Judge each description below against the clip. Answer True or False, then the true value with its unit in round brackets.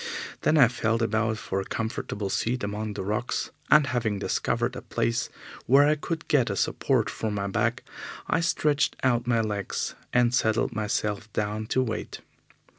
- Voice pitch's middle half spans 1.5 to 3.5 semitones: True (2.9 semitones)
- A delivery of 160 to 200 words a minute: True (170 wpm)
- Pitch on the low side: True (115 Hz)